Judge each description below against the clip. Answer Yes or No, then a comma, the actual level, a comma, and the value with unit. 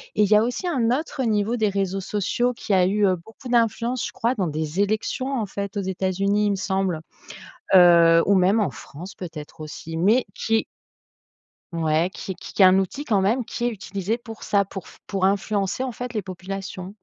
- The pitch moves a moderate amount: Yes, average, 3.3 semitones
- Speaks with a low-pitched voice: No, high, 200 Hz